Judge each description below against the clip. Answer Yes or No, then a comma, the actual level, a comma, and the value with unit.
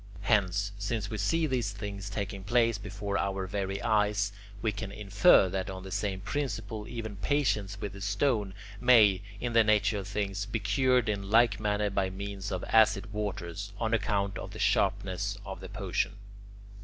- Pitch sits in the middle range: No, low, 100 Hz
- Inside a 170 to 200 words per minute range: Yes, average, 175 wpm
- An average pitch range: No, narrow, 1.8 semitones